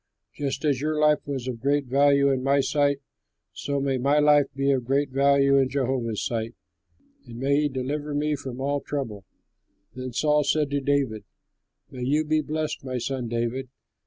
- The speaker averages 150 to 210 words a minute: Yes, average, 180 wpm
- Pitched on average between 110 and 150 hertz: Yes, medium, 140 Hz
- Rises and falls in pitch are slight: Yes, narrow, 2.0 semitones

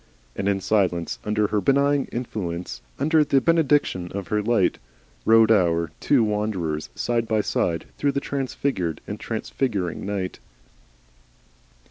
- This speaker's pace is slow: Yes, slow, 130 wpm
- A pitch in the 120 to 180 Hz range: No, low, 105 Hz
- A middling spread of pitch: No, wide, 6.6 semitones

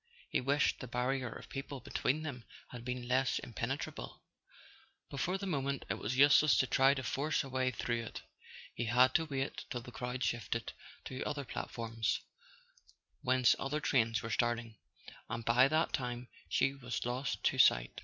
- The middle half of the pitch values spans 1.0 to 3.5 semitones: Yes, narrow, 2.5 semitones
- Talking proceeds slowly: No, average, 175 wpm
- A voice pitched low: Yes, low, 130 Hz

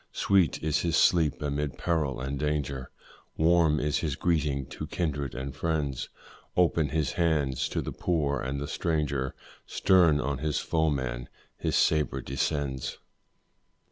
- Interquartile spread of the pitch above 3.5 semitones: No, average, 2.7 semitones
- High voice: No, very low, 75 Hz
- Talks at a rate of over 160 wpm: No, average, 140 wpm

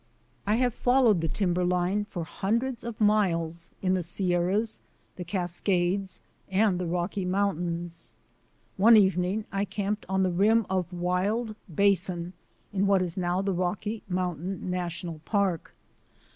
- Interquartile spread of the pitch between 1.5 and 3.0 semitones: Yes, narrow, 2.6 semitones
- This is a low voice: No, medium, 185 Hz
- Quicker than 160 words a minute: No, slow, 135 wpm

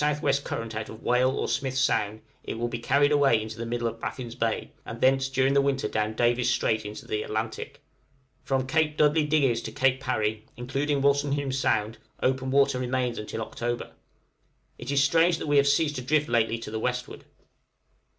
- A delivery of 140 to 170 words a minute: No, average, 190 wpm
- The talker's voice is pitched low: Yes, low, 130 Hz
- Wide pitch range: No, average, 3.4 semitones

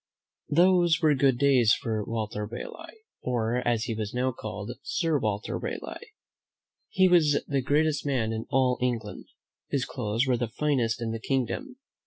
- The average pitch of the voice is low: Yes, low, 125 Hz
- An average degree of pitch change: Yes, average, 4.7 semitones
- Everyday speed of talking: Yes, average, 160 wpm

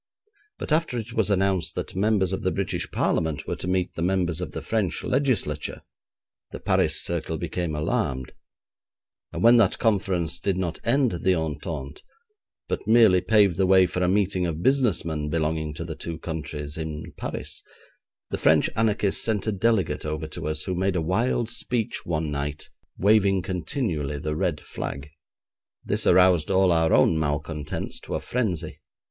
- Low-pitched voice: Yes, very low, 90 Hz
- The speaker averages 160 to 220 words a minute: Yes, average, 170 wpm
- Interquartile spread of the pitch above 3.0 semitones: Yes, average, 4.6 semitones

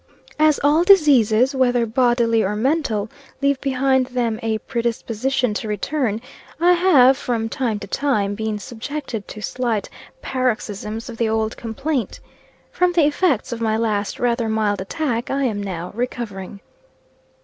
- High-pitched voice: Yes, high, 235 Hz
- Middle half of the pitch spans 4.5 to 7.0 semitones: No, average, 3.7 semitones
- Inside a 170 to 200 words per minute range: No, average, 145 wpm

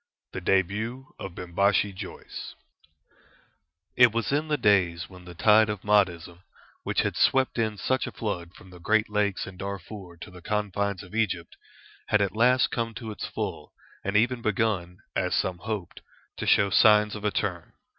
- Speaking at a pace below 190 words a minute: Yes, average, 175 wpm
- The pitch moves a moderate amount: Yes, average, 3.2 semitones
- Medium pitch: No, low, 100 Hz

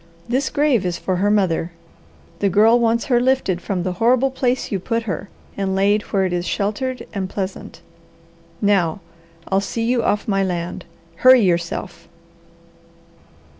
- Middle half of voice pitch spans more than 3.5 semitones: Yes, average, 4.2 semitones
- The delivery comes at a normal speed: Yes, average, 155 wpm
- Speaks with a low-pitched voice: No, high, 200 Hz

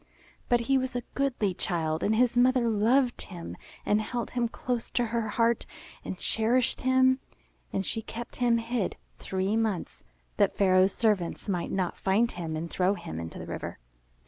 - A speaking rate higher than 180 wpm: No, average, 170 wpm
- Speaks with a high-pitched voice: Yes, high, 225 Hz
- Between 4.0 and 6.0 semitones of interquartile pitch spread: Yes, average, 4.3 semitones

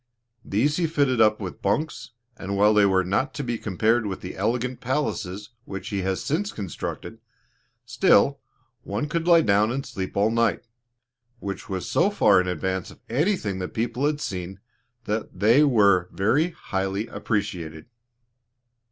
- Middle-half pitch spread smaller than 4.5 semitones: No, average, 5.3 semitones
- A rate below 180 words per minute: Yes, average, 160 wpm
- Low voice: Yes, low, 105 Hz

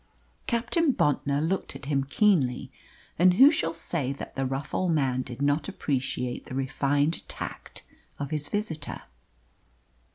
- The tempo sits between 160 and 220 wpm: No, average, 140 wpm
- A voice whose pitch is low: No, medium, 145 Hz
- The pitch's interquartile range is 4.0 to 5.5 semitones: Yes, average, 4.3 semitones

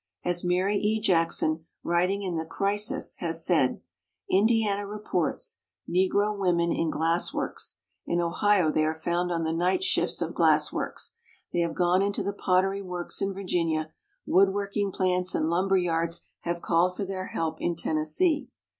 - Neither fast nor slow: Yes, average, 165 wpm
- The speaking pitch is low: No, medium, 180 Hz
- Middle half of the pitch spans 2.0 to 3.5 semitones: Yes, average, 2.9 semitones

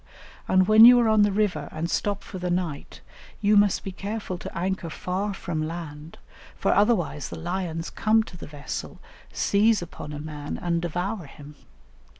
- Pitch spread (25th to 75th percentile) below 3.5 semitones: No, average, 4.1 semitones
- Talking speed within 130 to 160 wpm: No, average, 175 wpm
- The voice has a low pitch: No, medium, 180 Hz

